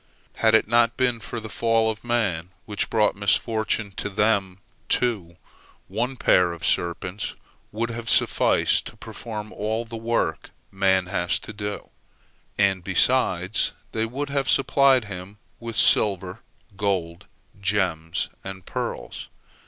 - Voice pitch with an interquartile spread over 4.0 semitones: No, average, 3.4 semitones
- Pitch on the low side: Yes, low, 105 Hz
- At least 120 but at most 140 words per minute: Yes, slow, 135 wpm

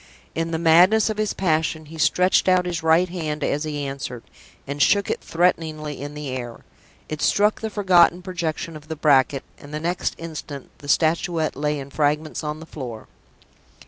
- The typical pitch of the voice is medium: Yes, medium, 160 Hz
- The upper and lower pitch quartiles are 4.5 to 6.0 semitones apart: No, average, 3.0 semitones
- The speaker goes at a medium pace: Yes, average, 180 wpm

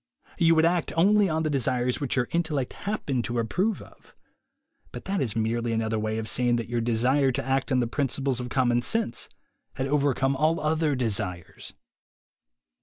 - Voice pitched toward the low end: Yes, low, 130 Hz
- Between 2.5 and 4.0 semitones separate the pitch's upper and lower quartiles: No, average, 4.6 semitones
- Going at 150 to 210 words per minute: Yes, average, 180 wpm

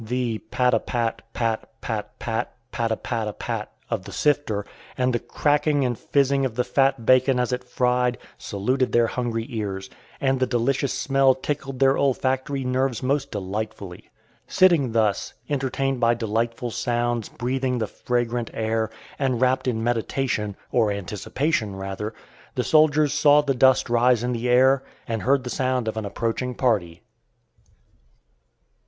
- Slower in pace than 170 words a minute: Yes, average, 155 wpm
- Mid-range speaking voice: No, low, 125 Hz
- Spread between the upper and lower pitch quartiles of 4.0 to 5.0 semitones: No, average, 2.9 semitones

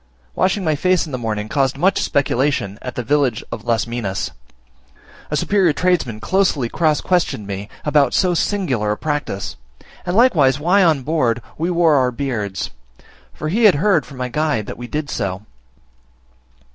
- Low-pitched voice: No, medium, 145 Hz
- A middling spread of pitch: No, wide, 6.4 semitones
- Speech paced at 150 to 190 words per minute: Yes, average, 170 wpm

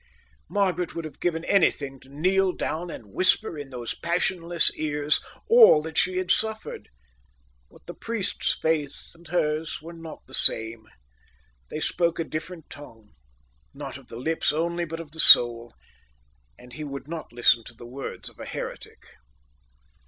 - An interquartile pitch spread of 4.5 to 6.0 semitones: No, average, 3.9 semitones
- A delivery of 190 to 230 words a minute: No, average, 160 wpm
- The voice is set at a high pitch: No, medium, 160 Hz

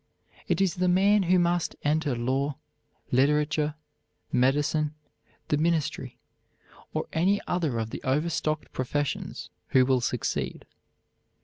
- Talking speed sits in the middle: No, slow, 115 wpm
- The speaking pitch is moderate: Yes, medium, 150 Hz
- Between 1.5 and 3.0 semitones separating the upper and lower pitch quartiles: No, average, 4.1 semitones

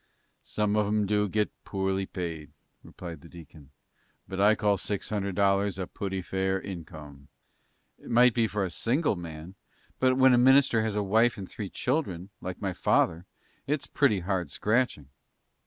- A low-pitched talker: Yes, low, 100 Hz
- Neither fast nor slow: Yes, average, 170 wpm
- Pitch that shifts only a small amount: No, average, 3.4 semitones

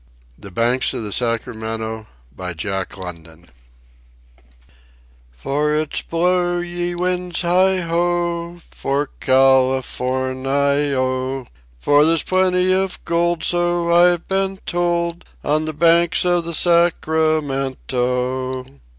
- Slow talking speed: Yes, slow, 105 wpm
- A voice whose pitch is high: No, medium, 155 Hz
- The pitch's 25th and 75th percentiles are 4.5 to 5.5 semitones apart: Yes, average, 5.1 semitones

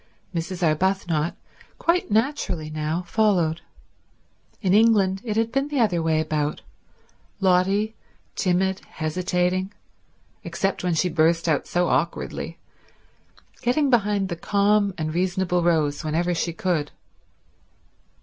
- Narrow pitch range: No, average, 3.8 semitones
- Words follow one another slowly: Yes, slow, 110 wpm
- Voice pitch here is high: No, medium, 180 Hz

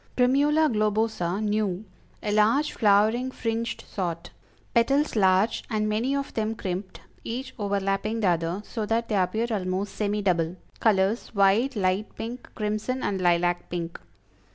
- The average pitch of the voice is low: No, high, 210 Hz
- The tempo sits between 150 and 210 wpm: No, average, 140 wpm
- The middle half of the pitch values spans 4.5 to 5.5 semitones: No, average, 3.2 semitones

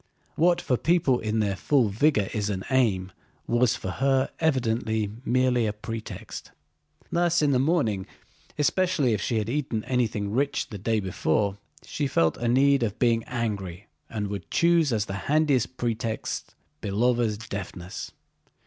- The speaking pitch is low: Yes, low, 115 Hz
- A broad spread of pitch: No, average, 4.6 semitones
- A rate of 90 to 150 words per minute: Yes, average, 145 wpm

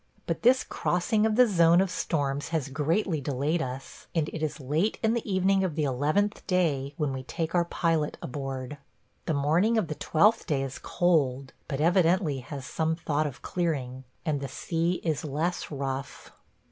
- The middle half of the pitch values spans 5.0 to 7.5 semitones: No, average, 4.3 semitones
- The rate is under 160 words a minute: No, average, 180 wpm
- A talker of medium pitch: Yes, medium, 155 Hz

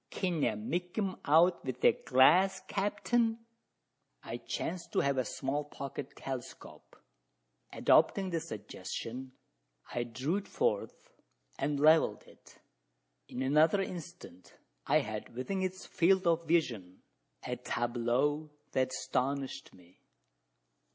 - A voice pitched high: No, medium, 145 Hz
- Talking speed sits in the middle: No, slow, 120 wpm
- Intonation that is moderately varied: No, wide, 5.8 semitones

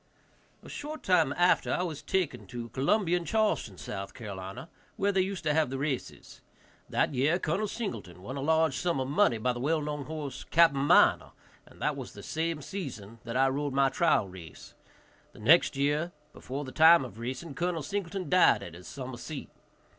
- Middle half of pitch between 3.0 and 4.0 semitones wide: No, average, 5.1 semitones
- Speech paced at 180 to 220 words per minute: Yes, average, 190 wpm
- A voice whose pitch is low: No, medium, 145 Hz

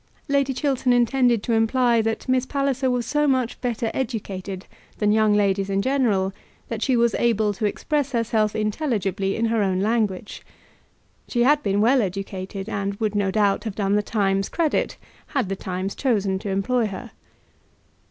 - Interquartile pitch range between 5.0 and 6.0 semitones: No, average, 4.1 semitones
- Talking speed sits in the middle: Yes, average, 170 wpm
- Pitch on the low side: No, high, 220 Hz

